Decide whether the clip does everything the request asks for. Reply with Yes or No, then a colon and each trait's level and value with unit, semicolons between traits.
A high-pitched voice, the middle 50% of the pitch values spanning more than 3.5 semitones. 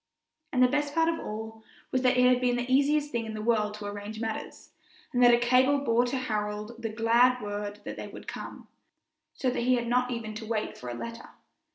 No: high, 235 Hz; average, 2.7 semitones